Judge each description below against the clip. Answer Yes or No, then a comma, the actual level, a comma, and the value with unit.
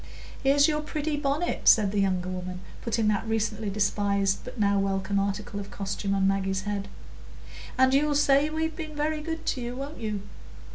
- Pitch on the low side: No, high, 215 Hz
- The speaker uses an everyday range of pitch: No, wide, 6.5 semitones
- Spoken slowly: No, average, 180 wpm